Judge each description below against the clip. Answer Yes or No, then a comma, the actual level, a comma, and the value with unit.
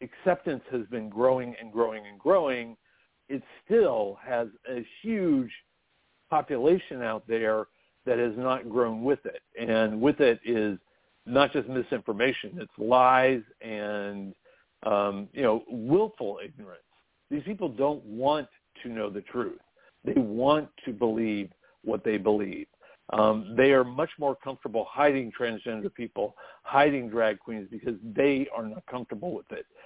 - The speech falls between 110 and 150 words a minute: Yes, average, 145 wpm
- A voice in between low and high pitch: No, low, 125 Hz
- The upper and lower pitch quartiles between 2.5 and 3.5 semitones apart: No, average, 4.6 semitones